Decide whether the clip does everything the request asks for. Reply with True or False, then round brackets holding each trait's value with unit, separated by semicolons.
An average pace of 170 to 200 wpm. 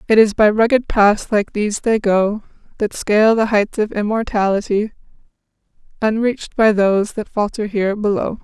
False (155 wpm)